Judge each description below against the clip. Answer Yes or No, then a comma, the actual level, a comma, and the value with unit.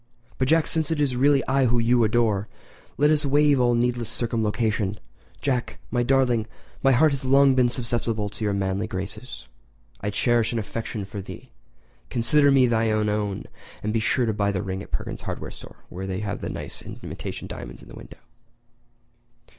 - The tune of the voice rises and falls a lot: No, average, 3.7 semitones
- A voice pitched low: Yes, low, 120 Hz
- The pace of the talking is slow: No, average, 175 wpm